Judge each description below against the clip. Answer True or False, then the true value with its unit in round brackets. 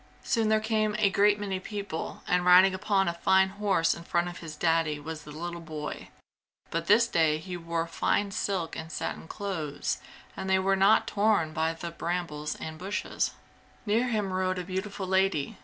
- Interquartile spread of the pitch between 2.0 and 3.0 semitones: False (3.5 semitones)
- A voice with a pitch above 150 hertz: True (185 Hz)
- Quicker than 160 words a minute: True (185 wpm)